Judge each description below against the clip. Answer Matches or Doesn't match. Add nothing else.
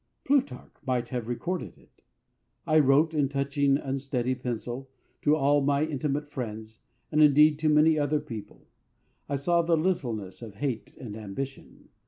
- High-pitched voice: Doesn't match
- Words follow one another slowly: Doesn't match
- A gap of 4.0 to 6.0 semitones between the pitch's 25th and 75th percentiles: Doesn't match